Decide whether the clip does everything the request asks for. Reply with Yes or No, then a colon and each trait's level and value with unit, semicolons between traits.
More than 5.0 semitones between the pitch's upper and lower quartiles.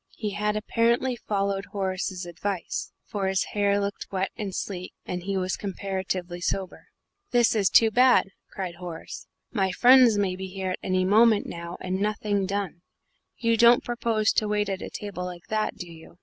No: narrow, 2.4 semitones